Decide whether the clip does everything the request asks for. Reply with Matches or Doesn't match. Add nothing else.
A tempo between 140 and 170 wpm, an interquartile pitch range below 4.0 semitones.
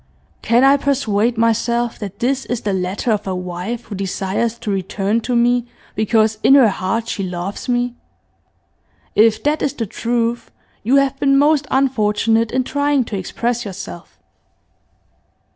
Matches